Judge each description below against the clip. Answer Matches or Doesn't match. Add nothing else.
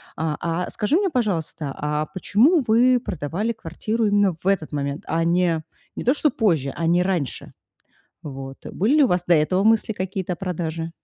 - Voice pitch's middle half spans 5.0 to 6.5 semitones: Matches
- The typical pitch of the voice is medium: Matches